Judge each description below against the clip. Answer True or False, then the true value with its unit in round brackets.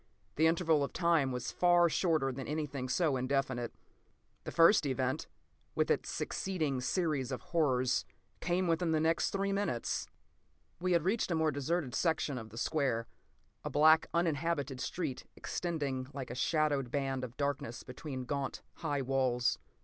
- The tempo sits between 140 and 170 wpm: True (155 wpm)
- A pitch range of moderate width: True (4.1 semitones)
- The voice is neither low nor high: True (145 Hz)